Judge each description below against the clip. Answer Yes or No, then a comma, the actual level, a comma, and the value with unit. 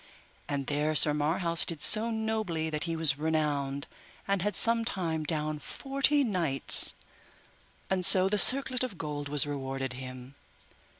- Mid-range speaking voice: Yes, medium, 160 Hz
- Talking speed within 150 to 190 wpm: No, average, 140 wpm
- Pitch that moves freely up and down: Yes, wide, 5.8 semitones